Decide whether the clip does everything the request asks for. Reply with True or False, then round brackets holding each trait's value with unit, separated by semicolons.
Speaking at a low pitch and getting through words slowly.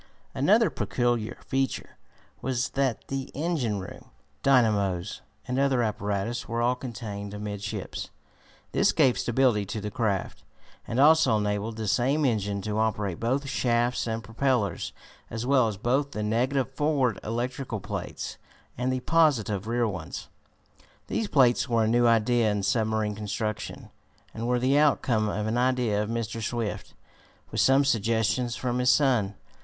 False (115 Hz; 150 wpm)